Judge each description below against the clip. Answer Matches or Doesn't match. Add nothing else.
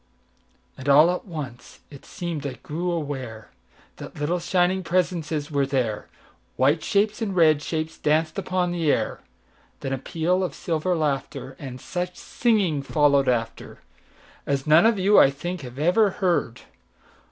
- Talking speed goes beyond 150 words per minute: Doesn't match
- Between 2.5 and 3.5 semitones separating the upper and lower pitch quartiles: Doesn't match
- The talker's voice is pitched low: Doesn't match